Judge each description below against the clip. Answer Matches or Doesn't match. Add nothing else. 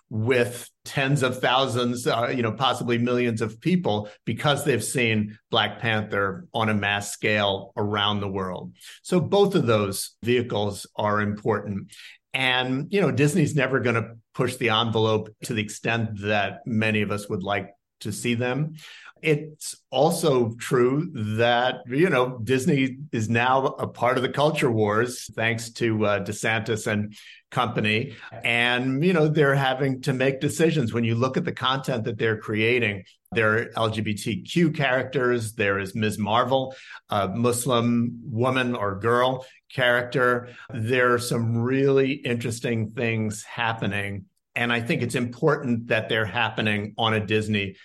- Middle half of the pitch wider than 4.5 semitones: Doesn't match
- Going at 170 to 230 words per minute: Doesn't match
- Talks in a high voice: Doesn't match